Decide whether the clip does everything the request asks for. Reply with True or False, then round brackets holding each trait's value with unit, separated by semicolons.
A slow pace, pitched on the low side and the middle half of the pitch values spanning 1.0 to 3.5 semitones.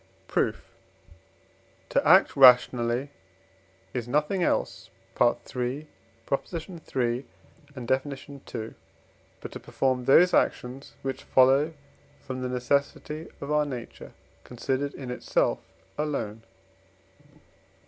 True (95 wpm; 130 Hz; 2.4 semitones)